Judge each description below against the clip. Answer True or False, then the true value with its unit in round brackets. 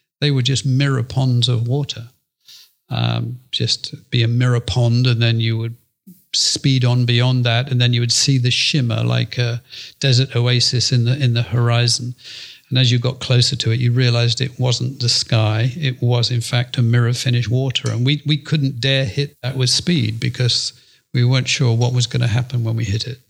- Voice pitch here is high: False (125 Hz)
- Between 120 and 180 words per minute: False (205 wpm)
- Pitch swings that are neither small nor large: False (1.7 semitones)